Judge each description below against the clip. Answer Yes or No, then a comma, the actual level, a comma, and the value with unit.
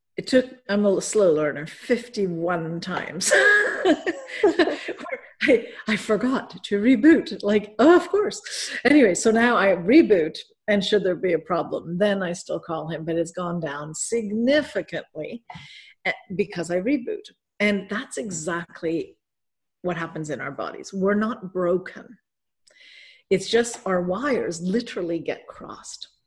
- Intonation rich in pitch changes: Yes, wide, 7.1 semitones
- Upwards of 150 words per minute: No, slow, 135 wpm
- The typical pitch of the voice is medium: No, high, 205 Hz